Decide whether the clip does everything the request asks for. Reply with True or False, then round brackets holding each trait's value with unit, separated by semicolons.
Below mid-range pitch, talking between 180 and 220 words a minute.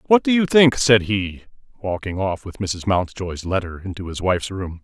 True (105 Hz; 200 wpm)